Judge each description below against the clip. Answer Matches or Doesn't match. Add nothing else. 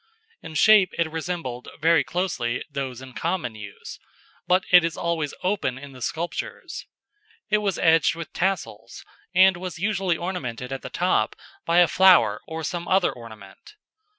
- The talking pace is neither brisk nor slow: Matches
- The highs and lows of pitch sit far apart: Matches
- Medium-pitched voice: Matches